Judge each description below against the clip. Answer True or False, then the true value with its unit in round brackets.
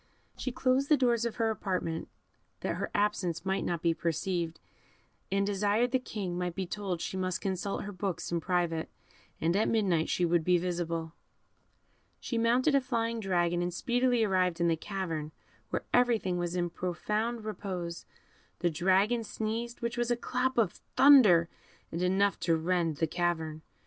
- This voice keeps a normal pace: True (170 wpm)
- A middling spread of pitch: True (4.9 semitones)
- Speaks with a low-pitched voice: False (190 Hz)